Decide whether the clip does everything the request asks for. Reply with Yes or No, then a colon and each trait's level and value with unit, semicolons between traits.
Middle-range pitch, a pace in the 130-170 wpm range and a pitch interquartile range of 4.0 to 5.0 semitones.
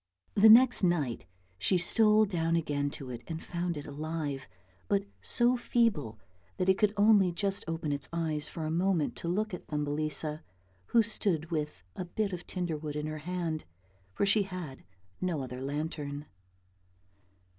Yes: medium, 165 Hz; average, 165 wpm; average, 4.4 semitones